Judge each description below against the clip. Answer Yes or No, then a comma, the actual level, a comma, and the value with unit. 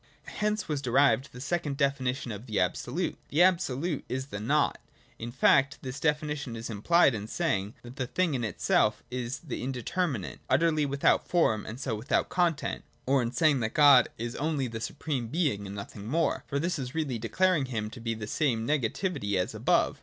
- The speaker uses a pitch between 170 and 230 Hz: No, low, 135 Hz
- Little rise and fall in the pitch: No, average, 5.0 semitones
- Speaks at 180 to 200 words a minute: Yes, average, 195 wpm